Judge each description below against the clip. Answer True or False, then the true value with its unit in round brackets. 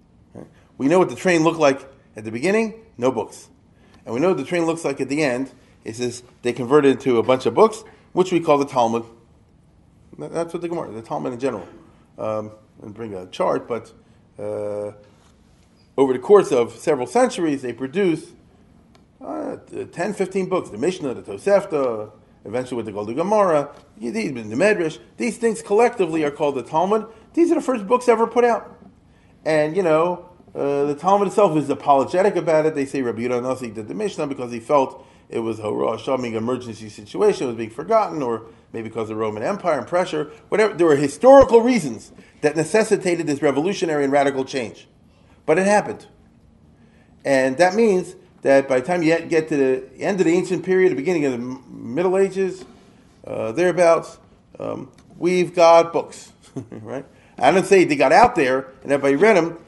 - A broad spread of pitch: True (7.0 semitones)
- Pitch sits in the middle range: True (150 Hz)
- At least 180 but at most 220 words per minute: True (190 wpm)